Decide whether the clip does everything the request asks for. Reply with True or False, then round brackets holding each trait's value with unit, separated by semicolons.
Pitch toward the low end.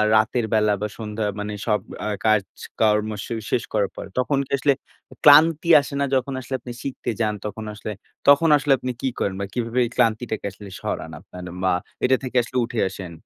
True (115 Hz)